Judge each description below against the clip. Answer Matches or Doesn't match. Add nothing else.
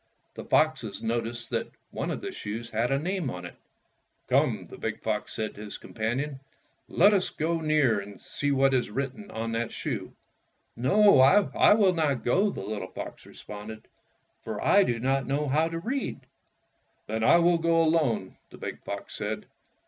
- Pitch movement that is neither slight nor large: Doesn't match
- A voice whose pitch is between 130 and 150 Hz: Matches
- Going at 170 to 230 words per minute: Matches